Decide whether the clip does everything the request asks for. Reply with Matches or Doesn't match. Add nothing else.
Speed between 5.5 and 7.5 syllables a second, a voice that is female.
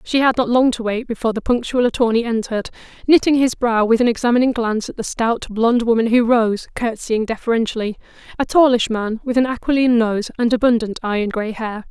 Matches